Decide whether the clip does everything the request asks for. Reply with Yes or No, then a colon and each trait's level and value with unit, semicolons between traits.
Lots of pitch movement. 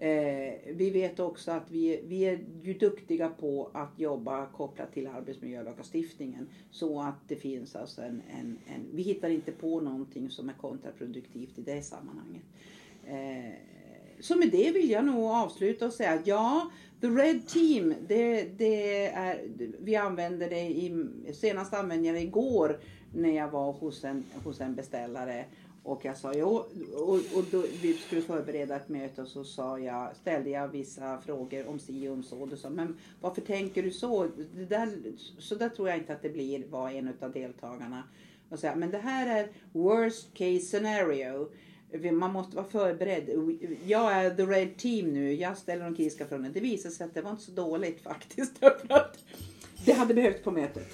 Yes: wide, 7.2 semitones